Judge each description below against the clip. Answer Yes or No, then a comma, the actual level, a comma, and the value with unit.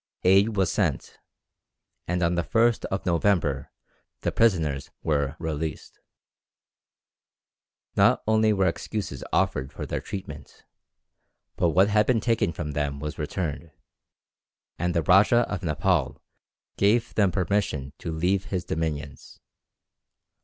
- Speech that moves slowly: Yes, slow, 125 wpm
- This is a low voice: Yes, very low, 90 Hz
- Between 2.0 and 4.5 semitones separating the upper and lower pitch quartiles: No, average, 4.9 semitones